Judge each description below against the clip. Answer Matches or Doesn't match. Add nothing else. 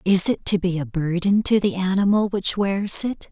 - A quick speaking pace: Matches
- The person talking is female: Matches